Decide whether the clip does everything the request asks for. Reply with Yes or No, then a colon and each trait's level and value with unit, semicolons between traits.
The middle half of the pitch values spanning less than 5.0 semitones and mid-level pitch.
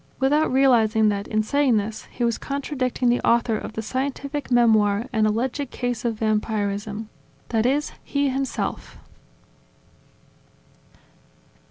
No: average, 3.6 semitones; high, 235 Hz